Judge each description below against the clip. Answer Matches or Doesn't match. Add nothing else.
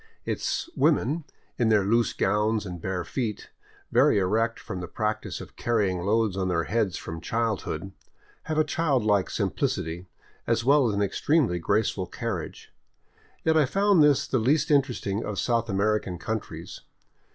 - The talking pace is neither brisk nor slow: Matches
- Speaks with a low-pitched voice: Matches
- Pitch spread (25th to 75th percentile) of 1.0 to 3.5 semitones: Doesn't match